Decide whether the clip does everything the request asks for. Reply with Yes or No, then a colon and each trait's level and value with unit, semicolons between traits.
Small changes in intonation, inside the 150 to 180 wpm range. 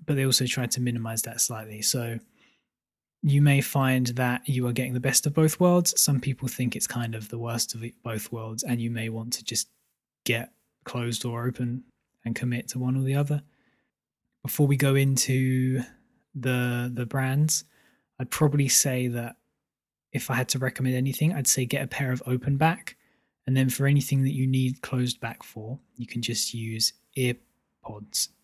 No: narrow, 2.2 semitones; average, 190 wpm